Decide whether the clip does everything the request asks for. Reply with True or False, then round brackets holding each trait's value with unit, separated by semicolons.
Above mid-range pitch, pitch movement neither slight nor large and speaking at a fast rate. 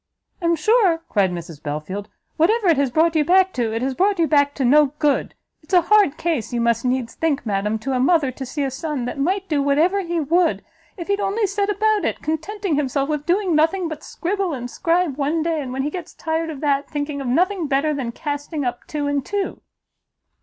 True (300 Hz; 4.7 semitones; 225 wpm)